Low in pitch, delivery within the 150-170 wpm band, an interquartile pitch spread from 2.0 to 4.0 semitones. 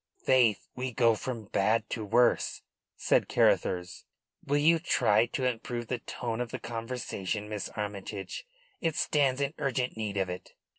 Yes: low, 115 Hz; average, 155 wpm; average, 3.6 semitones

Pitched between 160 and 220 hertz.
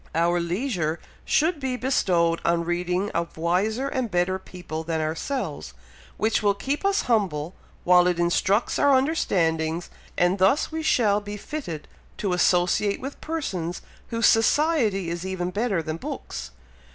Yes: medium, 185 Hz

